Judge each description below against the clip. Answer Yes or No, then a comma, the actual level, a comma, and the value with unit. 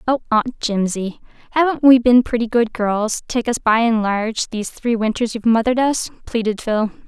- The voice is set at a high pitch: Yes, high, 230 Hz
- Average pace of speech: Yes, average, 185 wpm